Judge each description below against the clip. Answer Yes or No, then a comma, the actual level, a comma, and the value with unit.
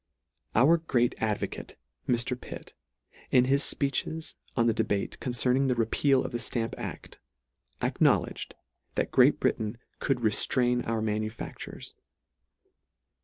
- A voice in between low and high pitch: No, low, 120 Hz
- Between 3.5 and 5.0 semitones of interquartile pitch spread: No, average, 2.8 semitones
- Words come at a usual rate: No, slow, 120 wpm